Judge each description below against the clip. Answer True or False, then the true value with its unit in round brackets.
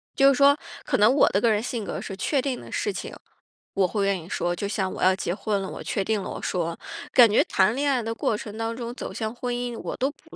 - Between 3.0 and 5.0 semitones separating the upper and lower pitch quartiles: True (4.1 semitones)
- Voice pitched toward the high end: True (220 Hz)